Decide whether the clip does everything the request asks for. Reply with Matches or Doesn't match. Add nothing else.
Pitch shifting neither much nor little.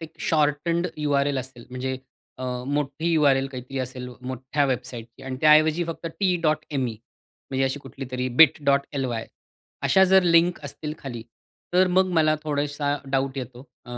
Matches